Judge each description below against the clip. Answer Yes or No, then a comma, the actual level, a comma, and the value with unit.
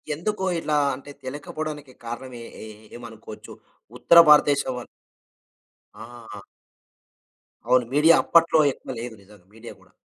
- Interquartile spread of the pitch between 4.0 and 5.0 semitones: Yes, average, 4.4 semitones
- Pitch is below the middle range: Yes, low, 130 Hz